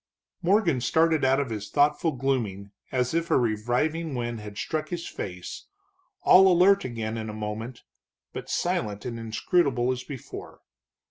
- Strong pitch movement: Yes, wide, 6.2 semitones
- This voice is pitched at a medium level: No, low, 125 Hz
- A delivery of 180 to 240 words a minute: No, average, 150 wpm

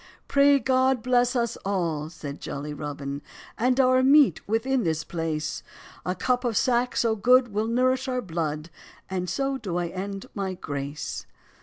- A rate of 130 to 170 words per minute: Yes, average, 160 wpm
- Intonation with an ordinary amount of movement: No, wide, 7.7 semitones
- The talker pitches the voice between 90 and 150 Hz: No, high, 215 Hz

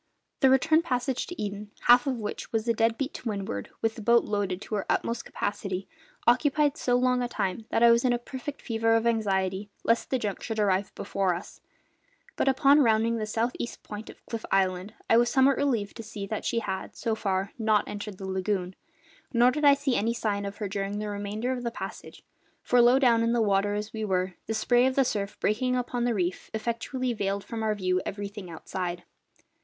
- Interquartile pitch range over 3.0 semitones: Yes, average, 3.4 semitones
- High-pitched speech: Yes, high, 220 Hz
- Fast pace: Yes, fast, 215 wpm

